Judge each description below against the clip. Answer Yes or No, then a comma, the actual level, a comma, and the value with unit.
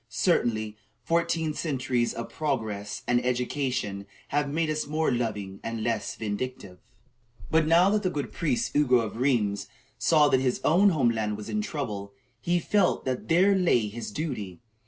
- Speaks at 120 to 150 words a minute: No, average, 160 wpm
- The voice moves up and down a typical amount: No, wide, 6.5 semitones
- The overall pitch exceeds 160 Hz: No, low, 130 Hz